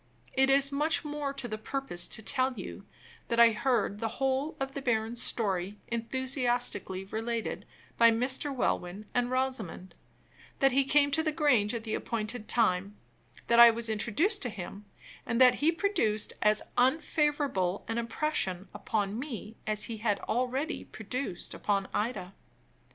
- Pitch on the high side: Yes, high, 235 Hz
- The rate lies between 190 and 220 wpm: No, average, 155 wpm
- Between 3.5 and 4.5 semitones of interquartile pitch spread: Yes, average, 4.2 semitones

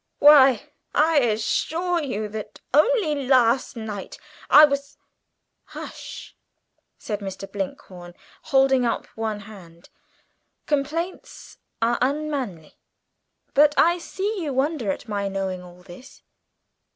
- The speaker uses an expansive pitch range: Yes, wide, 6.7 semitones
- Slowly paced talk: Yes, slow, 115 wpm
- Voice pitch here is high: Yes, very high, 255 Hz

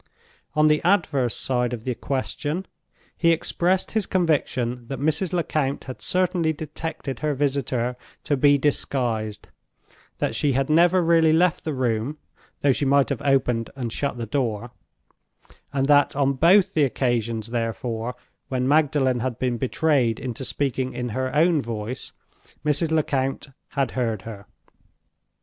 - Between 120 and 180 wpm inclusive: Yes, average, 145 wpm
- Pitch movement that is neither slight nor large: Yes, average, 4.0 semitones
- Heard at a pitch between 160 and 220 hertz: No, low, 135 Hz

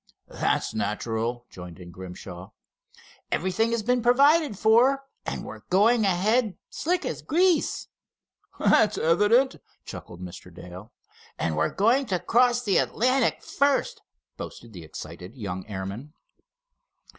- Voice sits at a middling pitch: No, high, 195 Hz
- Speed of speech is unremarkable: No, slow, 120 wpm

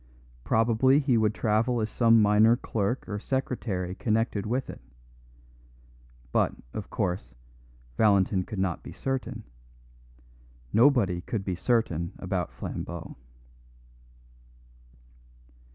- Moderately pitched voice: No, low, 110 Hz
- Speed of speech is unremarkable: No, slow, 105 wpm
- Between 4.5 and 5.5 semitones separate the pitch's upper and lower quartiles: No, average, 3.7 semitones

